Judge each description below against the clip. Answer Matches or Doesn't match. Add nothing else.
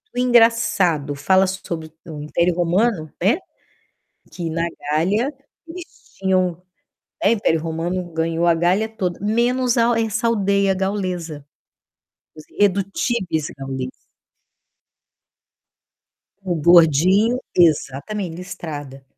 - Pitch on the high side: Doesn't match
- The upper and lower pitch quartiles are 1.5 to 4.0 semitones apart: Doesn't match